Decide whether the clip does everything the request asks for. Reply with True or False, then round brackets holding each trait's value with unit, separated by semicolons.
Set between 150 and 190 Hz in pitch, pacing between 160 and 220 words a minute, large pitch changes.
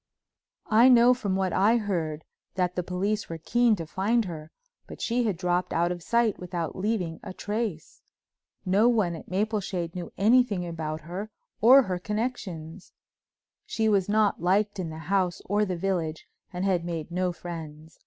False (185 Hz; 170 wpm; 3.9 semitones)